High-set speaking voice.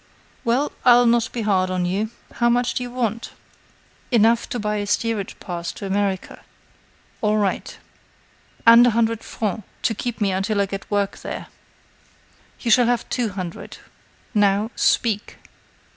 Yes: high, 215 Hz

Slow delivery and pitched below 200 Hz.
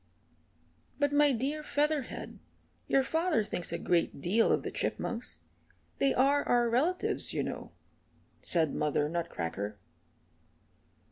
No: slow, 120 wpm; high, 245 Hz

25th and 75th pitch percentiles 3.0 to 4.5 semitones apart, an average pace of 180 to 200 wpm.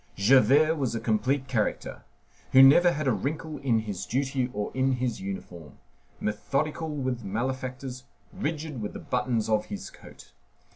No: average, 4.1 semitones; average, 150 wpm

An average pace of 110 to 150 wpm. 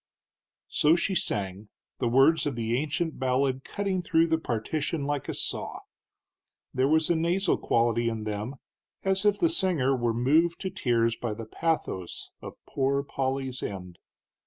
No: average, 160 wpm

